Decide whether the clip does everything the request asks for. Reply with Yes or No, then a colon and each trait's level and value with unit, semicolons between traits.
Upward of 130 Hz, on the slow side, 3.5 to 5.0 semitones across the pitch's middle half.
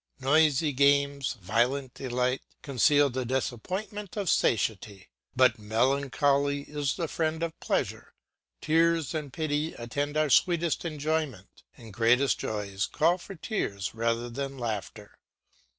Yes: medium, 140 Hz; slow, 120 wpm; average, 4.7 semitones